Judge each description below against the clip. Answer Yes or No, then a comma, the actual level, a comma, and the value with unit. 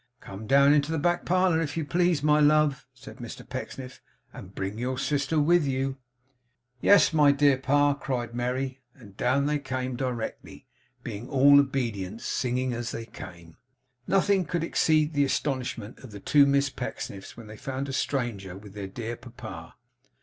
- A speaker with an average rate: Yes, average, 170 wpm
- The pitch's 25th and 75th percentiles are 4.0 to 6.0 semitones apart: No, average, 3.6 semitones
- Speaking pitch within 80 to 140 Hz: Yes, low, 135 Hz